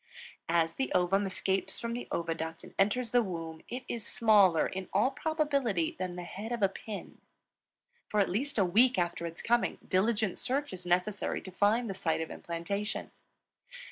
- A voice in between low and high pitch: No, high, 195 Hz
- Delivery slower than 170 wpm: No, average, 175 wpm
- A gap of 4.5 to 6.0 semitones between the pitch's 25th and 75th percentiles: Yes, average, 4.9 semitones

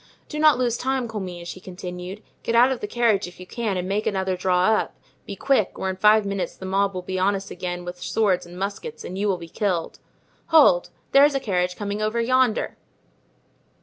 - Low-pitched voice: No, high, 200 Hz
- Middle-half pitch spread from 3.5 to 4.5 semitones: Yes, average, 4.2 semitones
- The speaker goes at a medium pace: No, fast, 215 wpm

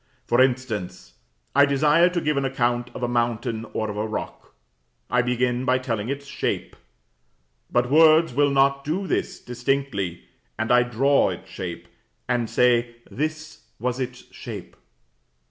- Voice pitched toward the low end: Yes, low, 125 Hz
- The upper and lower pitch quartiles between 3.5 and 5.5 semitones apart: No, average, 2.9 semitones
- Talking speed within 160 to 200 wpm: No, average, 150 wpm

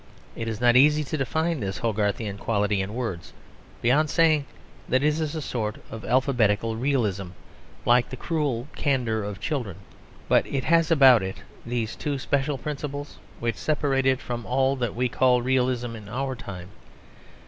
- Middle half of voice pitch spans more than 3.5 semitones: Yes, average, 4.0 semitones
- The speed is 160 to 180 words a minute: Yes, average, 165 wpm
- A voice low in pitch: Yes, low, 125 Hz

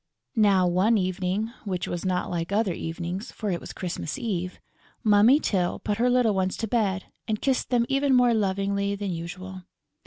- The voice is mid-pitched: No, high, 200 Hz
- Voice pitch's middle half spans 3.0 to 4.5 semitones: Yes, average, 3.4 semitones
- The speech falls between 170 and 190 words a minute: Yes, average, 180 wpm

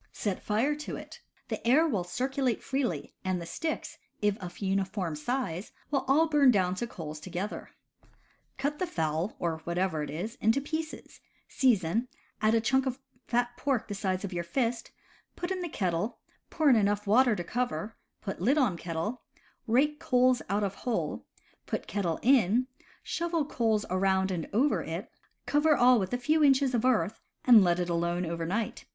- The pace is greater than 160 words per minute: Yes, average, 180 wpm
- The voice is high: Yes, high, 220 Hz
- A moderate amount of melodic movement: No, wide, 6.2 semitones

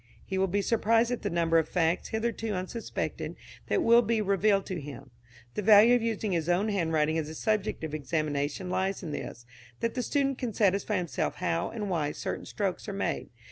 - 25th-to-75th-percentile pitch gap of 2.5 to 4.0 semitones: No, average, 5.3 semitones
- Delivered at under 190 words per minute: No, average, 200 wpm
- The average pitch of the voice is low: No, high, 190 Hz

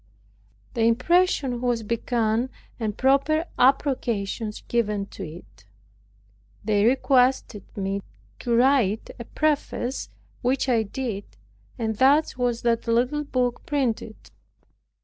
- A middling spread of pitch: Yes, average, 3.4 semitones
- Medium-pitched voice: No, high, 240 Hz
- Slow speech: Yes, slow, 110 wpm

